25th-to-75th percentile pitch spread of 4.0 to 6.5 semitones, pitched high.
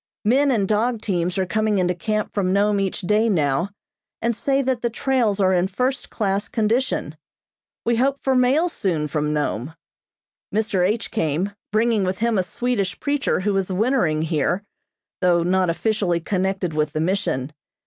Yes: average, 4.4 semitones; high, 200 Hz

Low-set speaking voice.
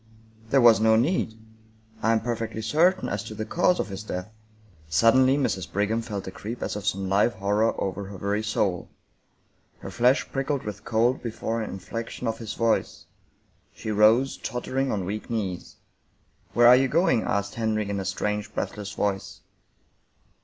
Yes: low, 110 Hz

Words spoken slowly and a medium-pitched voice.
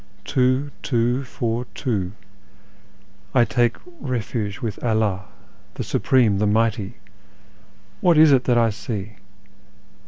No: slow, 115 wpm; low, 115 Hz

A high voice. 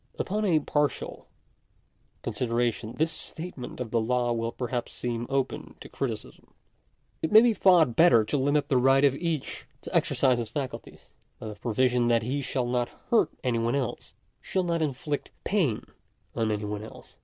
No: low, 130 Hz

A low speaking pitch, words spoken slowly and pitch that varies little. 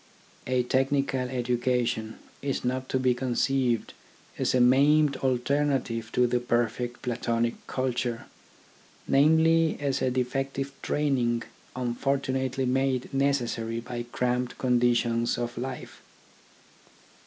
Yes: low, 125 Hz; slow, 110 wpm; narrow, 2.0 semitones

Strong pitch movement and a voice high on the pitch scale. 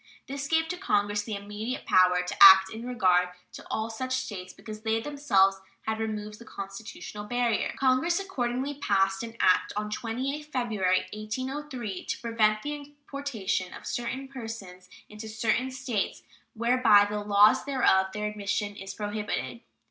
No: average, 4.1 semitones; high, 220 Hz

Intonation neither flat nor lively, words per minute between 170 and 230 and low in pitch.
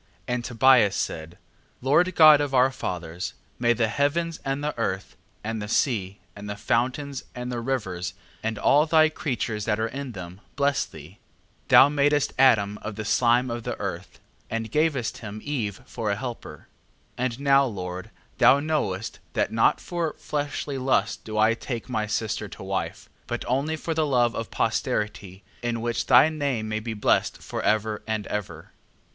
Yes: average, 4.9 semitones; average, 175 wpm; low, 120 Hz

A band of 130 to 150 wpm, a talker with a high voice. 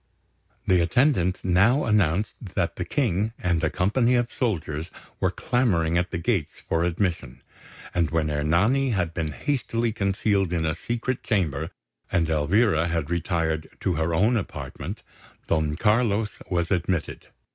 No: average, 145 wpm; very low, 90 Hz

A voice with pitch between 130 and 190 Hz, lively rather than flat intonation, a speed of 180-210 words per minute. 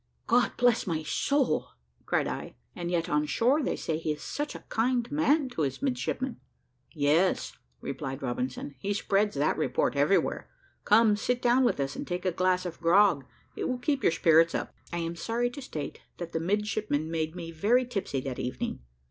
Yes: medium, 185 Hz; wide, 7.2 semitones; average, 190 wpm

